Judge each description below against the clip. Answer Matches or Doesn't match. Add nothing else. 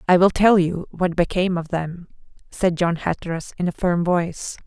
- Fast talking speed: Doesn't match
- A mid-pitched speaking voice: Matches